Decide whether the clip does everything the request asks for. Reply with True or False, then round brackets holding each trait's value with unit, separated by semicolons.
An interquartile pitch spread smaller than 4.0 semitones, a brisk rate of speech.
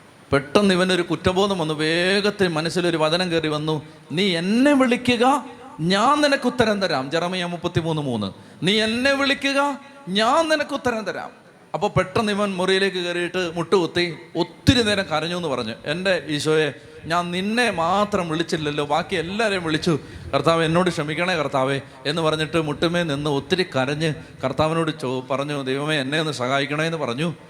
False (4.4 semitones; 145 wpm)